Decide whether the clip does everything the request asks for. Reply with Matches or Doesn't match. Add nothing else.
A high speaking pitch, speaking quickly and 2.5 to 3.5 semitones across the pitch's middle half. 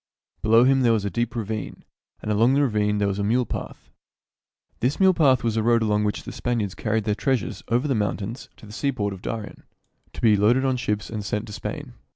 Doesn't match